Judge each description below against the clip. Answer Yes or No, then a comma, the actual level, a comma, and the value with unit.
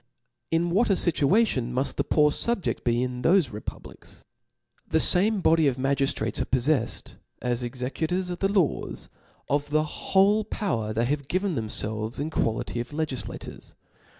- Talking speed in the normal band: Yes, average, 155 wpm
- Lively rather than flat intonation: Yes, wide, 6.5 semitones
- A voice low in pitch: No, medium, 145 Hz